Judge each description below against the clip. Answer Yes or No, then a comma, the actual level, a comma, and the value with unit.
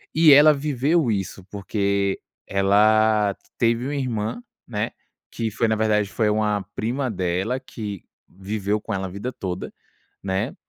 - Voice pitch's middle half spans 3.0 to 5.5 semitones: Yes, average, 3.4 semitones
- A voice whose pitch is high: No, low, 105 Hz